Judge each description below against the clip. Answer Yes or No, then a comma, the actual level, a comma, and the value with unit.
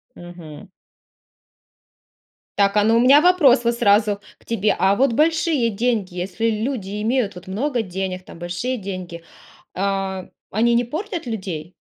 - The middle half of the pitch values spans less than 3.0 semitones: No, average, 4.5 semitones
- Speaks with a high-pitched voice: Yes, high, 210 Hz